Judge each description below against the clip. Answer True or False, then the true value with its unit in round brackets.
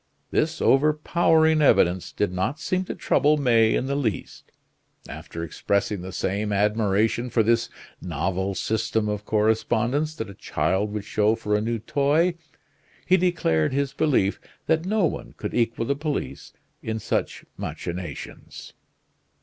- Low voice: True (115 Hz)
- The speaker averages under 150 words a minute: True (140 wpm)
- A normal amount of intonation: False (6.4 semitones)